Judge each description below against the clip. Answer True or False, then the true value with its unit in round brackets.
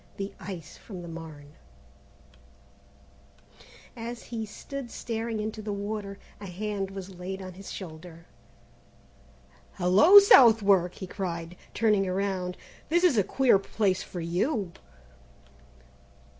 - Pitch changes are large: False (3.4 semitones)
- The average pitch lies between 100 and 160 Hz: False (195 Hz)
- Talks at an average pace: False (115 wpm)